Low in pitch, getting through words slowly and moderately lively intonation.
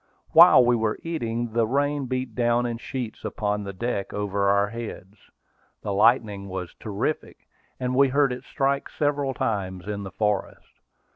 No: low, 115 Hz; average, 160 wpm; average, 4.1 semitones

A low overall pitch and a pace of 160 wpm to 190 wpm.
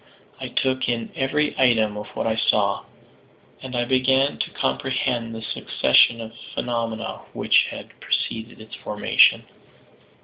No: low, 120 Hz; slow, 135 wpm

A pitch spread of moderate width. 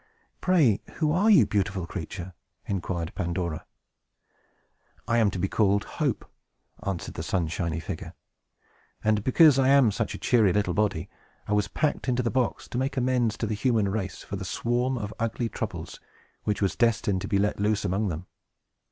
Yes: average, 4.2 semitones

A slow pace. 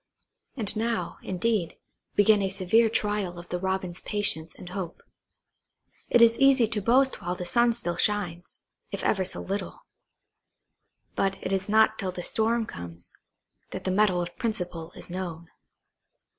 No: average, 155 wpm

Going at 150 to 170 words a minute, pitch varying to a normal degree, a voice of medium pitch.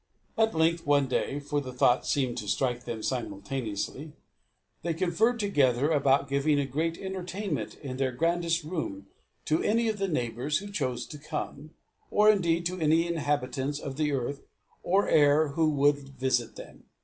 Yes: average, 165 wpm; average, 4.1 semitones; medium, 145 Hz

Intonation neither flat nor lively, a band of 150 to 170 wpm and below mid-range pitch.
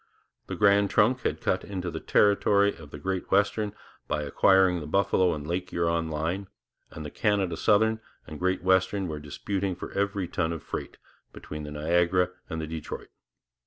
No: average, 3.7 semitones; average, 180 wpm; very low, 90 Hz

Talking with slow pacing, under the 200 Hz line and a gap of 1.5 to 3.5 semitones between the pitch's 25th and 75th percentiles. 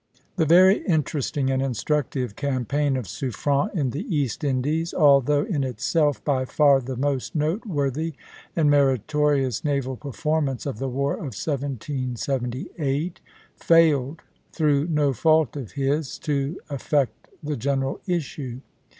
Yes: slow, 125 wpm; medium, 140 Hz; narrow, 2.4 semitones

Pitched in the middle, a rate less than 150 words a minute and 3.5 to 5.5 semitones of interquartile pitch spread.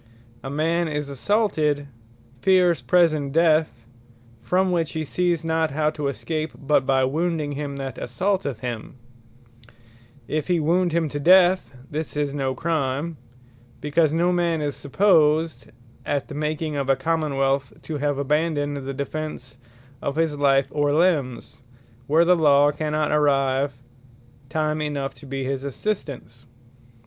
No: medium, 150 Hz; average, 140 wpm; average, 2.9 semitones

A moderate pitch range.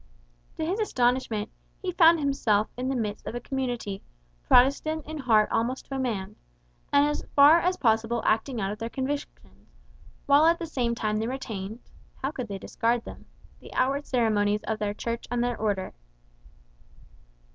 Yes: average, 4.3 semitones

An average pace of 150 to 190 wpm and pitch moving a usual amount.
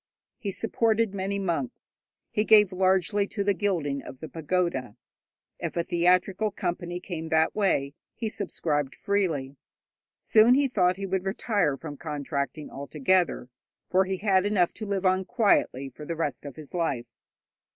Yes: average, 155 wpm; average, 4.5 semitones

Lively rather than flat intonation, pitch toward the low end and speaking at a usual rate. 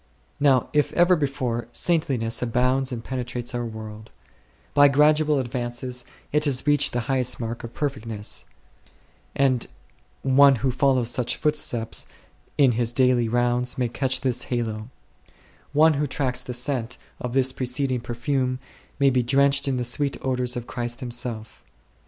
No: narrow, 2.4 semitones; low, 125 Hz; average, 145 wpm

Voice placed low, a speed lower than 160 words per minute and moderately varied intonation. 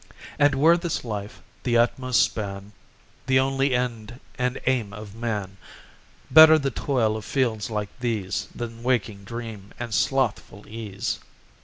Yes: low, 115 Hz; average, 140 wpm; average, 3.8 semitones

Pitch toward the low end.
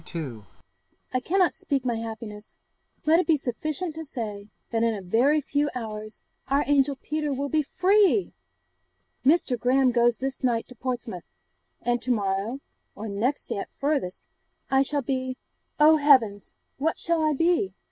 No: very high, 265 Hz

